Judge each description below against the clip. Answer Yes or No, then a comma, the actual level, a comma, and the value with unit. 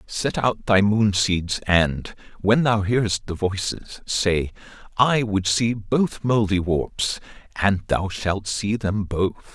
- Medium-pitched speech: No, low, 100 Hz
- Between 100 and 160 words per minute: Yes, average, 145 wpm